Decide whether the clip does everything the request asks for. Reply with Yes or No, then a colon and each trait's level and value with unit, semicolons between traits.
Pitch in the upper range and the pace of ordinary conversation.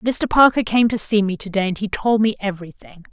No: high, 205 Hz; fast, 250 wpm